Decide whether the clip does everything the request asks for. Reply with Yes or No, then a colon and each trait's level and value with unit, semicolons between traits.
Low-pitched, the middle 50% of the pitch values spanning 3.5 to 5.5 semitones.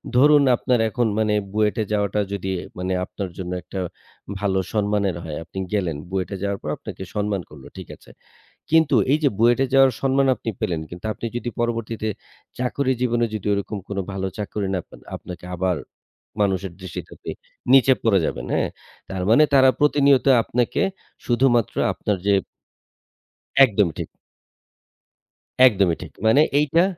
Yes: low, 105 Hz; average, 4.7 semitones